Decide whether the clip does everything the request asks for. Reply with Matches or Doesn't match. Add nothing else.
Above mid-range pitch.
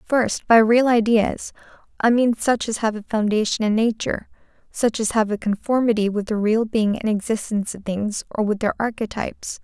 Matches